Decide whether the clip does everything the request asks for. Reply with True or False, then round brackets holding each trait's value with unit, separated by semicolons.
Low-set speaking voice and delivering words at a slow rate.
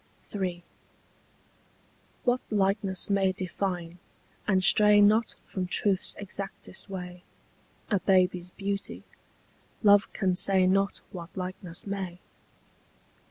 False (190 Hz; 100 wpm)